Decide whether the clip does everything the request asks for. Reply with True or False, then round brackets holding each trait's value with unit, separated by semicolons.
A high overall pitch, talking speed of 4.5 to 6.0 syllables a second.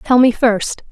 False (235 Hz; 3.6 syllables/s)